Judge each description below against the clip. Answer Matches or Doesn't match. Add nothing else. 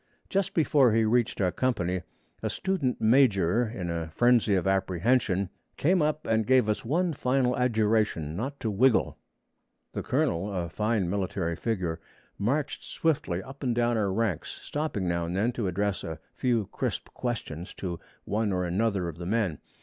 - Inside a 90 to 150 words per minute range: Doesn't match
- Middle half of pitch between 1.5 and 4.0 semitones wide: Doesn't match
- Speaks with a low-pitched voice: Matches